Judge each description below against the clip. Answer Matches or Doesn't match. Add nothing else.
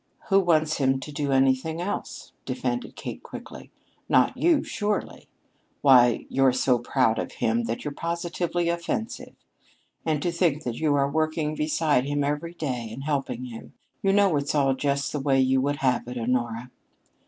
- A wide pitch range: Doesn't match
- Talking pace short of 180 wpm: Matches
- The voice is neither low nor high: Matches